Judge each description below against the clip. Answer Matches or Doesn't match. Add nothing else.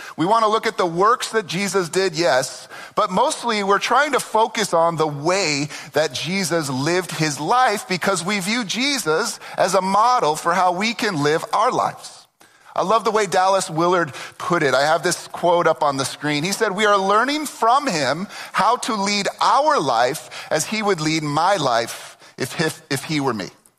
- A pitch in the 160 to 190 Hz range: Matches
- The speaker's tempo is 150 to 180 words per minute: Doesn't match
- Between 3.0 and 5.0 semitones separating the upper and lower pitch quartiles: Doesn't match